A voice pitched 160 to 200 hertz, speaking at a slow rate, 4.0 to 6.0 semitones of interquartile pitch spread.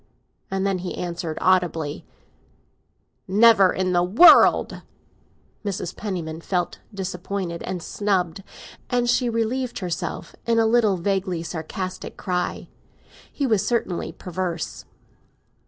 No: medium, 185 Hz; slow, 110 wpm; average, 3.1 semitones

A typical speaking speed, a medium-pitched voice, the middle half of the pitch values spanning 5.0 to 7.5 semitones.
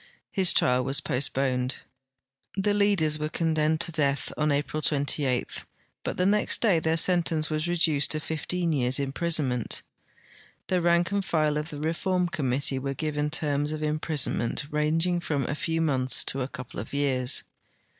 No: average, 160 wpm; medium, 155 Hz; average, 3.3 semitones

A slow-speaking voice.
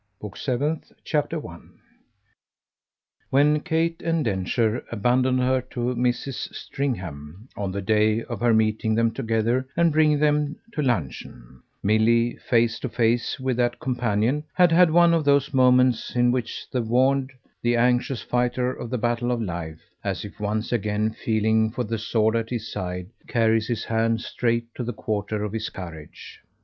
No: average, 160 wpm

